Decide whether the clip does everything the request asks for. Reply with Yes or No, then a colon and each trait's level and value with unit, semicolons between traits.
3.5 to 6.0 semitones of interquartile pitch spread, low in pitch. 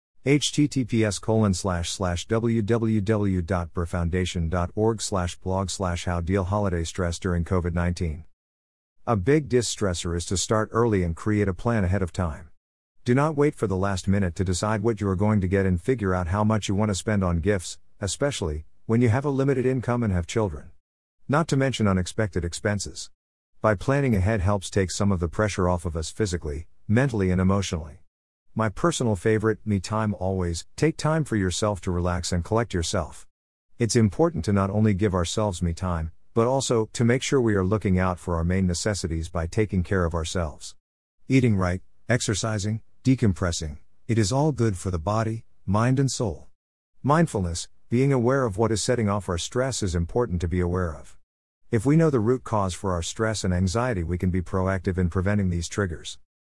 Yes: average, 4.2 semitones; low, 100 Hz